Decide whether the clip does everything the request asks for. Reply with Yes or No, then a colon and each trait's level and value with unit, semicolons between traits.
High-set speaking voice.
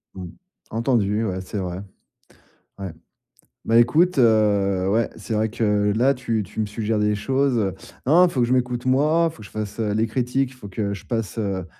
No: low, 110 Hz